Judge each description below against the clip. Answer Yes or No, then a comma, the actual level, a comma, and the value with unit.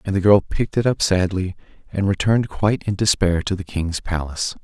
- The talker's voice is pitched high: No, very low, 95 Hz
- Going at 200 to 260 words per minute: Yes, fast, 205 wpm